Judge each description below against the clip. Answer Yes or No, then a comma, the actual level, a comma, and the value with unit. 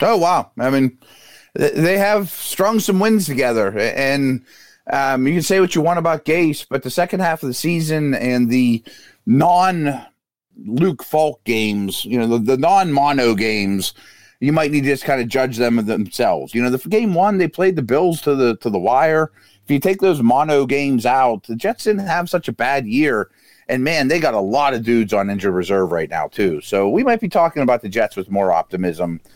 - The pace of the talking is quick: Yes, fast, 215 wpm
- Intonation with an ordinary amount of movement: No, wide, 6.4 semitones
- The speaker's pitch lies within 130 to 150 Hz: Yes, medium, 140 Hz